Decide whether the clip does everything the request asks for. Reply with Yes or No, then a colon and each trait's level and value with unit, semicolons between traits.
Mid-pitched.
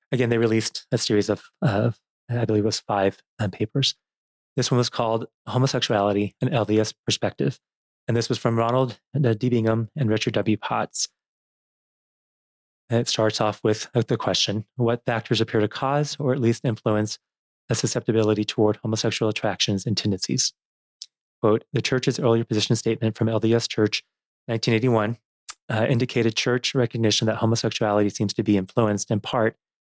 No: low, 115 Hz